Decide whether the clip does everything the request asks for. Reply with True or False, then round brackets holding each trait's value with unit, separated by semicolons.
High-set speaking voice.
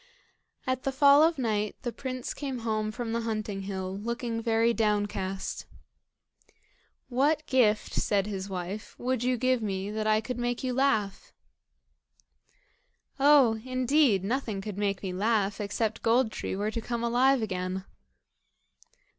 True (225 Hz)